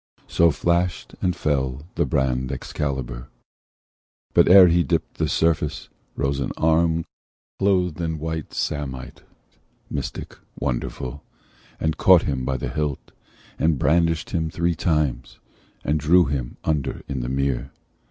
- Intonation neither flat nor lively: Yes, average, 3.8 semitones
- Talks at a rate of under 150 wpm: Yes, slow, 135 wpm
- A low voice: Yes, very low, 75 Hz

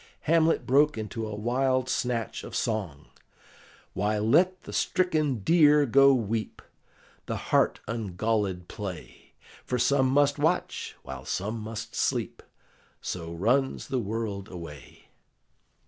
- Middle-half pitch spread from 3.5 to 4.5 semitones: No, average, 4.9 semitones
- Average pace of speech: No, slow, 120 wpm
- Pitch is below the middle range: Yes, low, 115 Hz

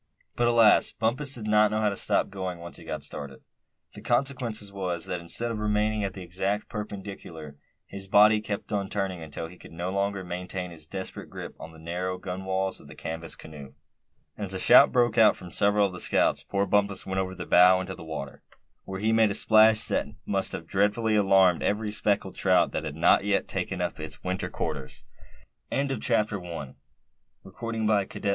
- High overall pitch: No, very low, 95 Hz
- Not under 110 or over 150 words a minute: No, average, 200 wpm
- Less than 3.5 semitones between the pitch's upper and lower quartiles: Yes, average, 3.0 semitones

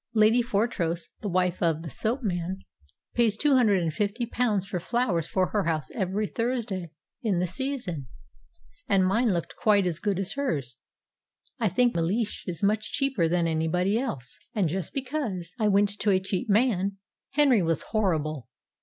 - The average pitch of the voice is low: No, high, 195 Hz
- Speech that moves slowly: No, average, 170 wpm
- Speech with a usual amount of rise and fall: Yes, average, 4.8 semitones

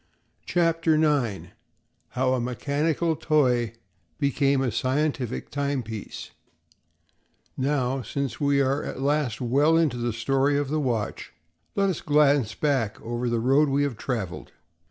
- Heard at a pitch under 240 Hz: Yes, low, 135 Hz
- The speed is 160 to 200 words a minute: No, slow, 135 wpm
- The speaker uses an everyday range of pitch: Yes, average, 3.2 semitones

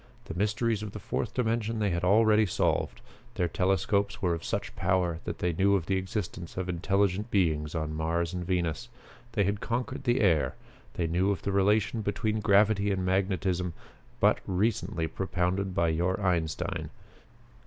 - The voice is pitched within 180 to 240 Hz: No, very low, 95 Hz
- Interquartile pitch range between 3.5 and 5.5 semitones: No, average, 3.0 semitones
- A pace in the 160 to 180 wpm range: Yes, average, 165 wpm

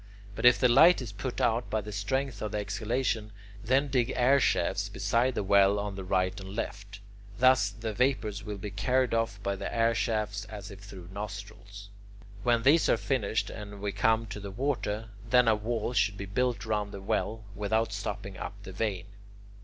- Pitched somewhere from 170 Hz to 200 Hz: No, low, 105 Hz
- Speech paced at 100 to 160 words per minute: No, average, 195 wpm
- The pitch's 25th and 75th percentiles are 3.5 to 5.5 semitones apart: No, average, 2.9 semitones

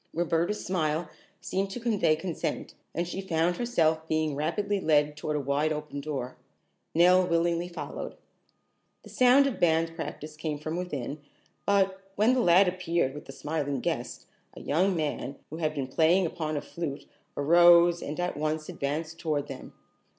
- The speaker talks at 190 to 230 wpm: No, average, 165 wpm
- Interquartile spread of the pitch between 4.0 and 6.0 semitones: No, average, 2.9 semitones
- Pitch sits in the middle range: Yes, medium, 160 Hz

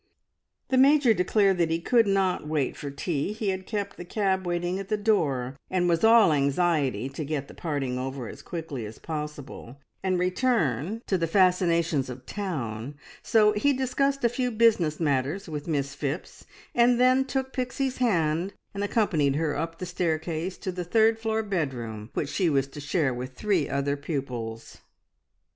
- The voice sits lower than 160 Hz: No, medium, 170 Hz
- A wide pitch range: Yes, wide, 6.8 semitones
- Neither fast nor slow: Yes, average, 175 wpm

